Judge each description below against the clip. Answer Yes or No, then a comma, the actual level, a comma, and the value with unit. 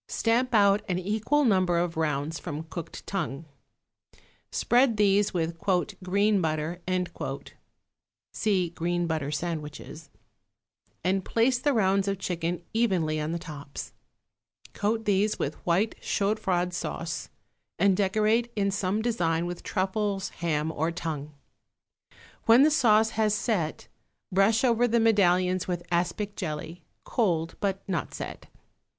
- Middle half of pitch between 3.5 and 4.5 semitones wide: Yes, average, 4.2 semitones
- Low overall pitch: No, medium, 185 Hz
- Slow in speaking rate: Yes, slow, 130 wpm